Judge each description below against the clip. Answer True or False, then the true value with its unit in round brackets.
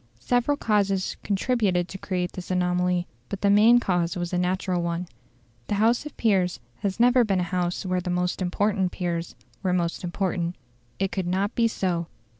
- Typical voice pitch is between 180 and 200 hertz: True (185 Hz)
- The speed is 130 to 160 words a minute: False (180 wpm)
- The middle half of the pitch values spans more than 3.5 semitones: False (2.4 semitones)